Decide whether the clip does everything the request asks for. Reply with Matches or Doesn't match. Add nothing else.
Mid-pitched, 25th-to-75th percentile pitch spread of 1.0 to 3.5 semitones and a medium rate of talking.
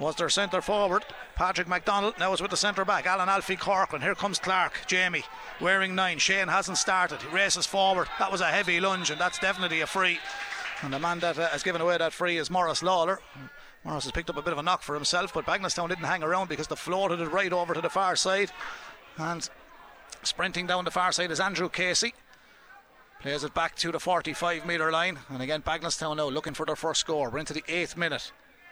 Doesn't match